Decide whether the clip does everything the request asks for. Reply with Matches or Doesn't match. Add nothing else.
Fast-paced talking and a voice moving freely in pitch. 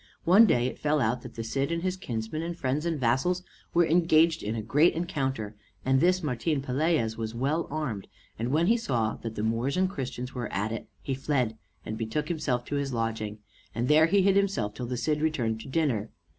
Matches